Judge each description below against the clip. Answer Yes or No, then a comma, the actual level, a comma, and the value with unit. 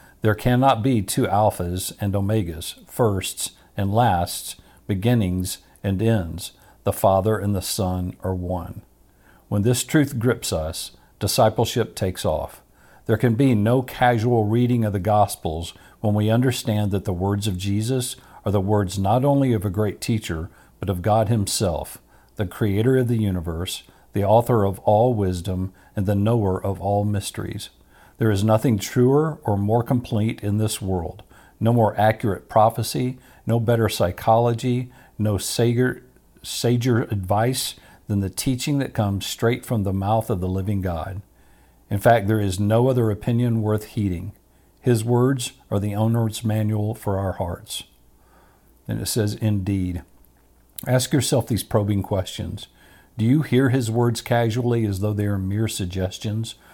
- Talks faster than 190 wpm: No, average, 155 wpm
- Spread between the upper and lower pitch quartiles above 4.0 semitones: No, average, 3.5 semitones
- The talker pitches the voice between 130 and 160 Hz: No, low, 105 Hz